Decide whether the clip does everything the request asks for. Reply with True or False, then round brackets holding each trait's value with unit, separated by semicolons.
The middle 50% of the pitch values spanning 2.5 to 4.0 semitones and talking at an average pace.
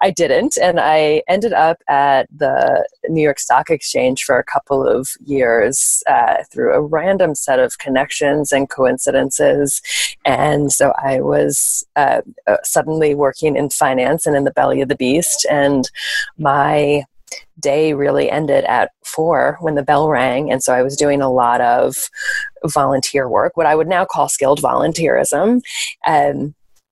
True (3.4 semitones; 160 wpm)